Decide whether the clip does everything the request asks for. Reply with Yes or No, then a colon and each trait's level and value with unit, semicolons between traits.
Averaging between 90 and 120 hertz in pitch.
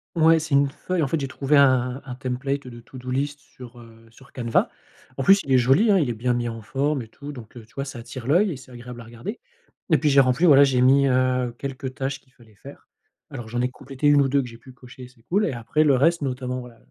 No: low, 130 Hz